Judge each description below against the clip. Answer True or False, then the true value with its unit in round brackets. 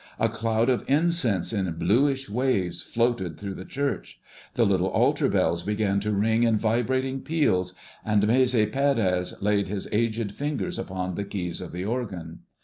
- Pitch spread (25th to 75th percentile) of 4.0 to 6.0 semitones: True (4.9 semitones)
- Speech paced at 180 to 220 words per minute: False (160 wpm)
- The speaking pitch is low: True (105 Hz)